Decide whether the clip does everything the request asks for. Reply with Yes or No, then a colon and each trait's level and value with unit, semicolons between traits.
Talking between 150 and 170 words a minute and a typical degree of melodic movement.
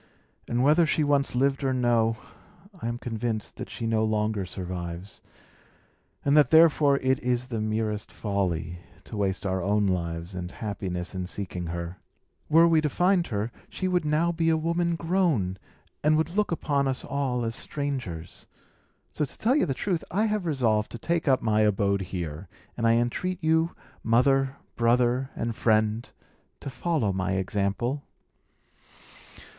No: average, 160 wpm; wide, 7.1 semitones